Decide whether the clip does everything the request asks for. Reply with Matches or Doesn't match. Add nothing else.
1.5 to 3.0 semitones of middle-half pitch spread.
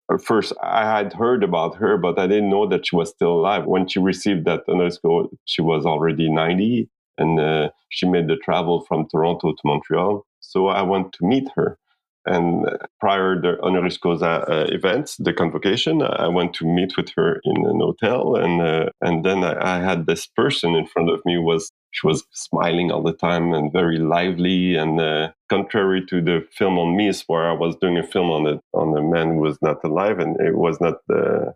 Matches